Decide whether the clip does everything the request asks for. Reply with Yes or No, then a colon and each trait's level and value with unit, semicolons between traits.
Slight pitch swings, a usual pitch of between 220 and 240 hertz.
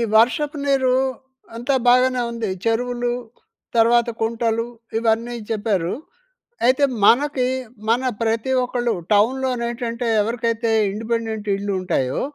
Yes: narrow, 1.9 semitones; high, 235 Hz